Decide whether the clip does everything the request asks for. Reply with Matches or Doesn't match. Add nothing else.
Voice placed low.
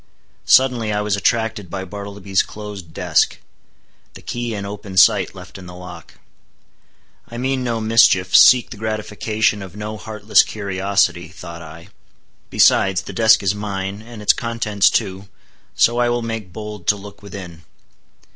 Matches